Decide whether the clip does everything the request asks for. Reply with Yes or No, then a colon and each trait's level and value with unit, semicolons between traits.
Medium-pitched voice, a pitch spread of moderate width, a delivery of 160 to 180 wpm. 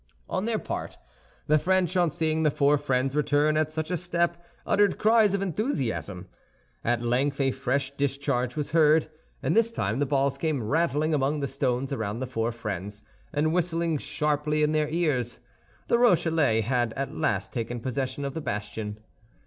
Yes: medium, 145 Hz; average, 4.2 semitones; average, 175 wpm